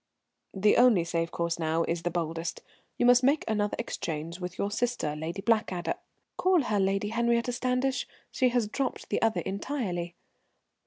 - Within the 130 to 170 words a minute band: Yes, average, 165 wpm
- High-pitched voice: Yes, high, 205 Hz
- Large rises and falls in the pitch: Yes, wide, 6.2 semitones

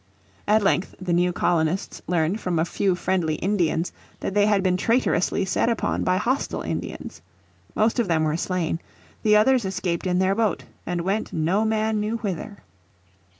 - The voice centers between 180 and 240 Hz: Yes, high, 190 Hz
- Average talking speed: Yes, average, 170 wpm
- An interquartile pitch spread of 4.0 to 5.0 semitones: No, average, 3.4 semitones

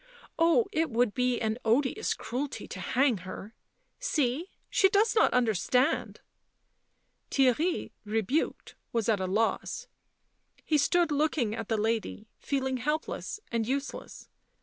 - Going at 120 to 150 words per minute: Yes, slow, 135 wpm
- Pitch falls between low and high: No, very high, 255 Hz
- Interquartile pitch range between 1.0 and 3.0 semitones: No, wide, 5.6 semitones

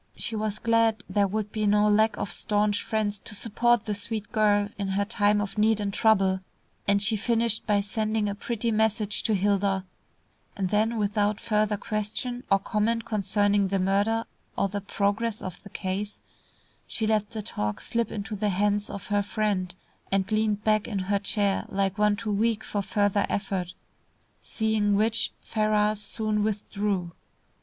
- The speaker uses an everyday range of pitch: No, narrow, 1.4 semitones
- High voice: Yes, high, 210 Hz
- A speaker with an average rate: Yes, average, 170 wpm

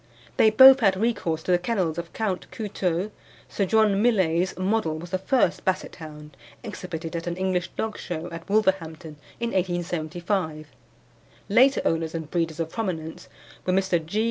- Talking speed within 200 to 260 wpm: No, average, 160 wpm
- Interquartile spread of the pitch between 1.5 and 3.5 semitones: No, average, 3.9 semitones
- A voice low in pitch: No, medium, 180 Hz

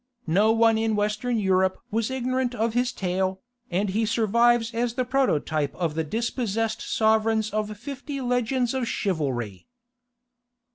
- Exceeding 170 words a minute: No, average, 140 wpm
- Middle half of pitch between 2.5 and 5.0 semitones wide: Yes, average, 4.0 semitones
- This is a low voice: No, high, 225 Hz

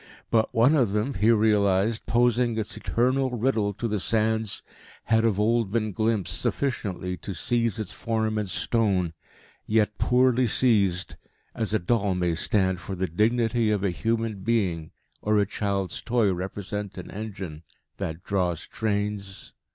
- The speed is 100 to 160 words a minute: Yes, average, 150 wpm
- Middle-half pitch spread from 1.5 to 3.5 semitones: Yes, average, 2.9 semitones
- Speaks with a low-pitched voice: Yes, low, 105 Hz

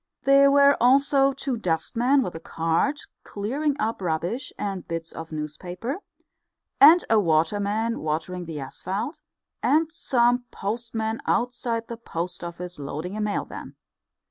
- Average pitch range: No, wide, 7.1 semitones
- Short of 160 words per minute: Yes, average, 140 wpm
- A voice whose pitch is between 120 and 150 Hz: No, high, 215 Hz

